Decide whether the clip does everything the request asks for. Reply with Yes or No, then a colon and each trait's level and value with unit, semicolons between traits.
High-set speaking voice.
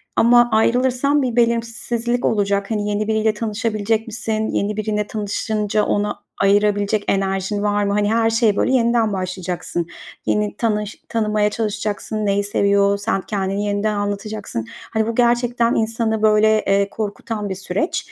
Yes: high, 215 Hz